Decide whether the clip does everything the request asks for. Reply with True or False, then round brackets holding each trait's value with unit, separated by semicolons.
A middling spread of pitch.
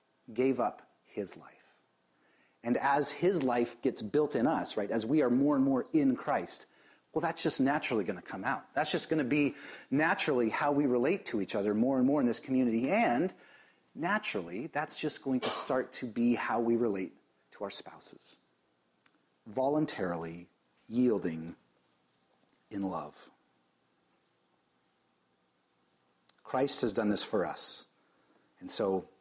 False (7.8 semitones)